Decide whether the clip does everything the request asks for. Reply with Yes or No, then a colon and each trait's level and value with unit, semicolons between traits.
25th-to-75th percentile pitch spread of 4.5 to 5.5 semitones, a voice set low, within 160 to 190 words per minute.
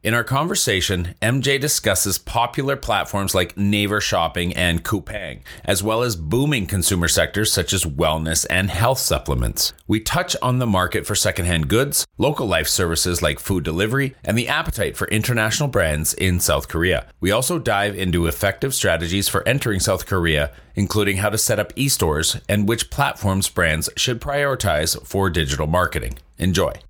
Yes: average, 4.8 semitones; low, 100 Hz; average, 165 wpm